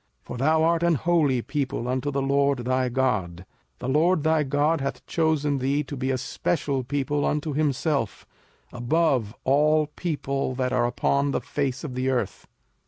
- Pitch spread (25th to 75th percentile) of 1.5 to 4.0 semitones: Yes, average, 2.8 semitones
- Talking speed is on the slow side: No, average, 170 wpm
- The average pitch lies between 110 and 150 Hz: Yes, medium, 140 Hz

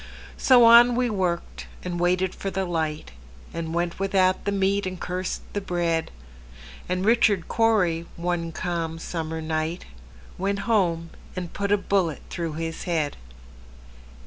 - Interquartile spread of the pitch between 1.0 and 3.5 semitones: Yes, average, 3.2 semitones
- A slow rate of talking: Yes, slow, 130 wpm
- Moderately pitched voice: Yes, medium, 175 Hz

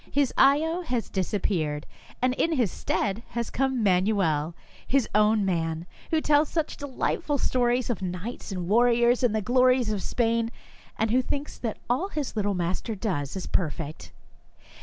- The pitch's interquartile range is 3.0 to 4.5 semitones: No, average, 5.3 semitones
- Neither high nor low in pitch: No, high, 225 Hz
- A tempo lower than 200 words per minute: Yes, average, 160 wpm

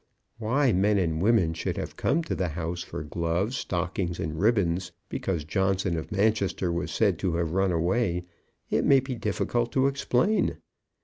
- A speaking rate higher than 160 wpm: Yes, average, 170 wpm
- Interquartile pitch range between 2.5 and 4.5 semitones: No, average, 5.0 semitones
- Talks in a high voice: No, very low, 95 Hz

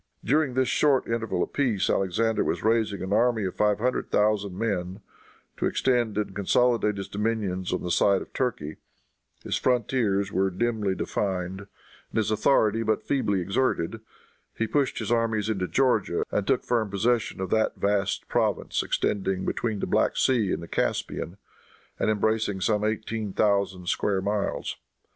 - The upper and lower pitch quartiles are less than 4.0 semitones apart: Yes, average, 2.9 semitones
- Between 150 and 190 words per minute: Yes, average, 160 wpm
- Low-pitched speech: Yes, low, 105 Hz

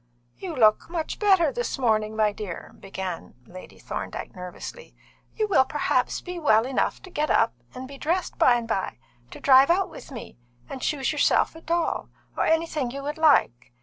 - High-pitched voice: Yes, very high, 275 Hz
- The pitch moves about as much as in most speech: No, wide, 7.0 semitones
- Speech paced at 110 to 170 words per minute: No, average, 180 wpm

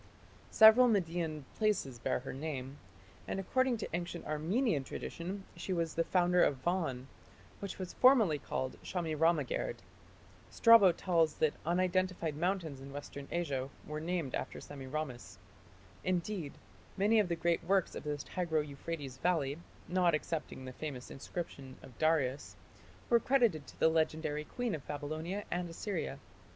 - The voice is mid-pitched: Yes, medium, 165 Hz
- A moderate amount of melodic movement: Yes, average, 4.2 semitones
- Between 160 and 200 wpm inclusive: No, average, 140 wpm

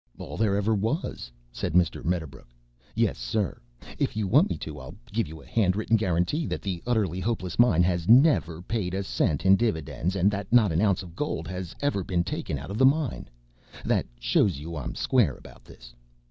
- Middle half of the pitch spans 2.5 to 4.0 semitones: No, average, 5.0 semitones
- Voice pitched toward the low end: Yes, very low, 95 Hz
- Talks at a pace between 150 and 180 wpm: No, average, 200 wpm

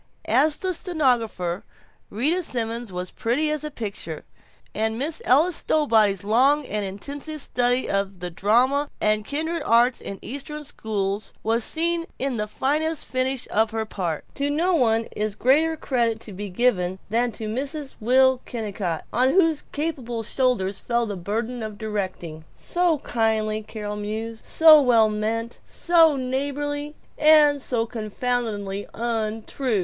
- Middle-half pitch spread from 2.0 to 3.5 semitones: No, average, 5.2 semitones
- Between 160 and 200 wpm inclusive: No, average, 145 wpm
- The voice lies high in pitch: Yes, high, 235 Hz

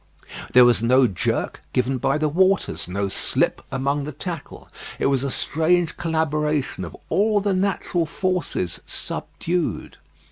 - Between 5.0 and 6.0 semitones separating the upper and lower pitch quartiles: Yes, wide, 5.4 semitones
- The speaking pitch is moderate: Yes, medium, 150 Hz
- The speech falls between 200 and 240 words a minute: No, average, 140 wpm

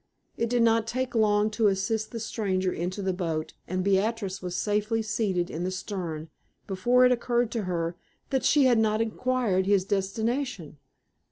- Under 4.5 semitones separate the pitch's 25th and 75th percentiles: Yes, average, 3.6 semitones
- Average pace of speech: Yes, average, 170 wpm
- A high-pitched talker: Yes, high, 210 Hz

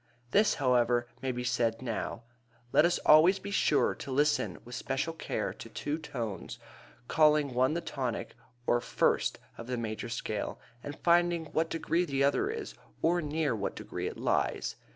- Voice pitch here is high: No, medium, 145 Hz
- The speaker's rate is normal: Yes, average, 170 wpm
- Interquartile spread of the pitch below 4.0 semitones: No, average, 5.0 semitones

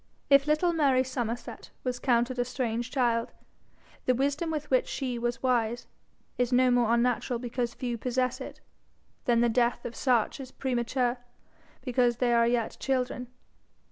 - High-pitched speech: Yes, high, 245 Hz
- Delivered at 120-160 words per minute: Yes, average, 155 wpm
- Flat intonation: Yes, narrow, 1.5 semitones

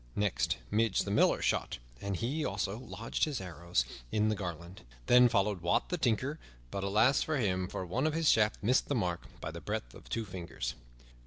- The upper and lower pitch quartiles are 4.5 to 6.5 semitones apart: Yes, average, 5.0 semitones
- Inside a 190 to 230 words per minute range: Yes, average, 195 wpm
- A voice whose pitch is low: Yes, low, 105 Hz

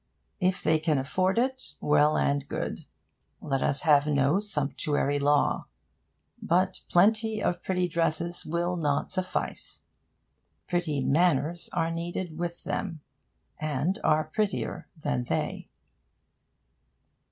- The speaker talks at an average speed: No, slow, 115 wpm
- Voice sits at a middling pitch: Yes, medium, 165 Hz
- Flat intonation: No, average, 3.7 semitones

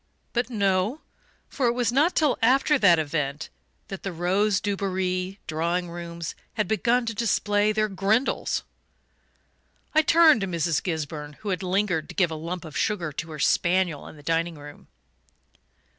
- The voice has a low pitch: No, medium, 185 Hz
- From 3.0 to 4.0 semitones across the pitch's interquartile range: No, average, 4.6 semitones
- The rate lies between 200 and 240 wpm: No, average, 160 wpm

